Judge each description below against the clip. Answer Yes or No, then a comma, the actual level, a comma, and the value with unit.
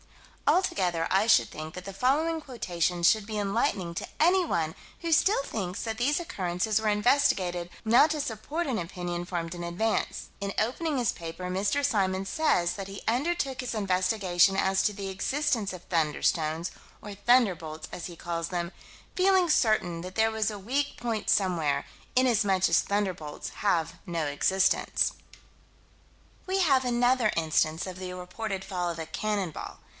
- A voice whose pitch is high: Yes, high, 195 Hz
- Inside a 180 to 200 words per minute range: No, average, 160 wpm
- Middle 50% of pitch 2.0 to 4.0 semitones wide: No, wide, 5.4 semitones